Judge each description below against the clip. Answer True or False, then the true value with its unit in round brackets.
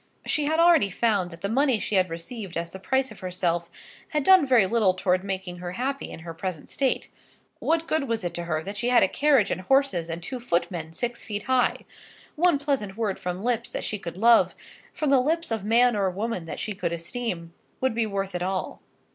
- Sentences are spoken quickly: True (225 wpm)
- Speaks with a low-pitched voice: False (210 Hz)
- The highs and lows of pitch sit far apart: True (6.0 semitones)